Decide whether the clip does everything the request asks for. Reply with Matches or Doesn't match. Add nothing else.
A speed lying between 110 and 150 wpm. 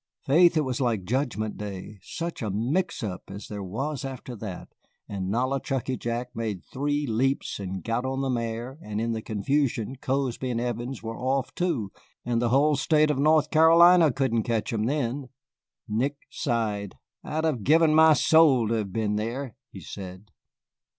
Doesn't match